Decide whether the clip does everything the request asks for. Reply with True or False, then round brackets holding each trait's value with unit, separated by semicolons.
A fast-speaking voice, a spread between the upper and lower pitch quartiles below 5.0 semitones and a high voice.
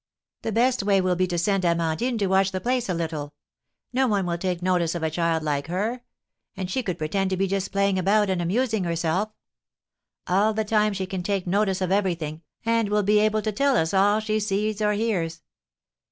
True (210 wpm; 3.4 semitones; 195 Hz)